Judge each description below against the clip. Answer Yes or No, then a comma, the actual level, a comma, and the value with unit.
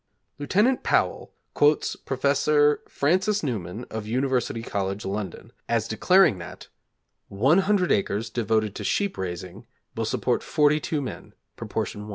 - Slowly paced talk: Yes, slow, 125 wpm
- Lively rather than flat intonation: Yes, wide, 6.5 semitones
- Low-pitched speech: Yes, low, 125 Hz